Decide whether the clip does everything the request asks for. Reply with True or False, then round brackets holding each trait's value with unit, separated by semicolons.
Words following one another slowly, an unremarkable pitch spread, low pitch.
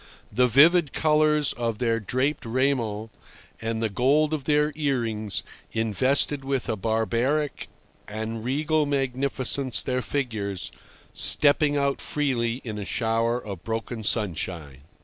True (125 wpm; 4.1 semitones; 125 Hz)